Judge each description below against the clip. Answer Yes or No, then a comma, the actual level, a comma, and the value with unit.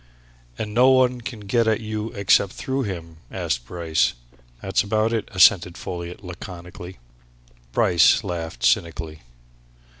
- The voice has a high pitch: No, very low, 95 Hz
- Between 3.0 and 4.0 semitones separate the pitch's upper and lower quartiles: No, average, 4.6 semitones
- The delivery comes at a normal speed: No, slow, 120 wpm